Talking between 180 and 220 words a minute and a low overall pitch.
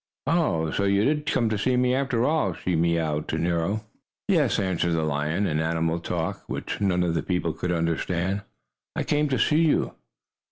Yes: average, 190 wpm; very low, 90 Hz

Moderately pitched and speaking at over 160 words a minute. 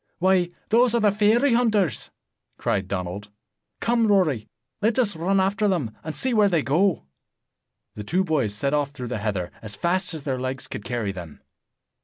Yes: medium, 165 Hz; average, 180 wpm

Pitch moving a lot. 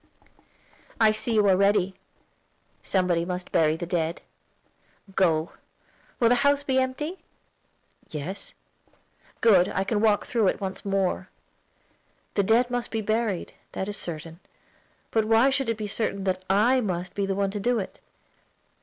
No: average, 3.7 semitones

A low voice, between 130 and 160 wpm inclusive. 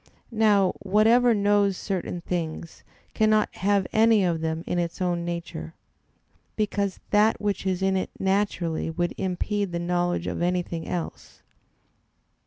No: medium, 185 Hz; slow, 135 wpm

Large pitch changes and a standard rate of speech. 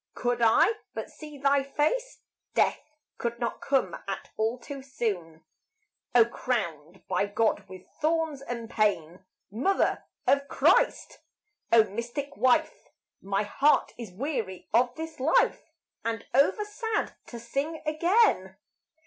No: wide, 5.7 semitones; slow, 130 wpm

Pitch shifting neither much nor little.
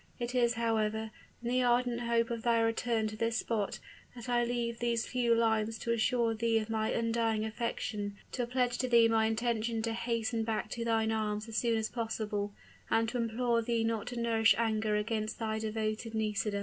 No: narrow, 1.3 semitones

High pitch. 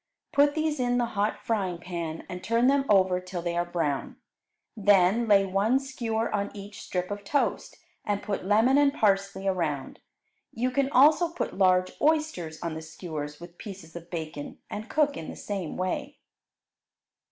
Yes: high, 200 Hz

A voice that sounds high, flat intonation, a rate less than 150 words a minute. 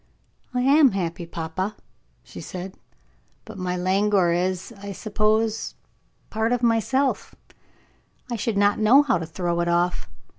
No: high, 200 Hz; average, 4.1 semitones; average, 140 wpm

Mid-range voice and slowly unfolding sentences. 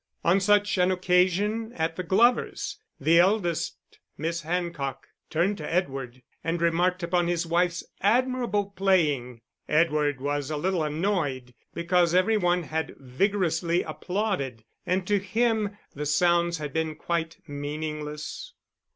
Yes: medium, 170 Hz; slow, 130 wpm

